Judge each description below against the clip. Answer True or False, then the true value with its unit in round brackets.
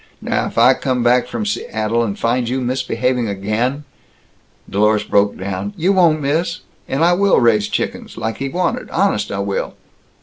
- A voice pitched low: True (120 Hz)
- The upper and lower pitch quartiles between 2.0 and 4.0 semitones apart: False (5.1 semitones)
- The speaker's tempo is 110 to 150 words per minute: False (175 wpm)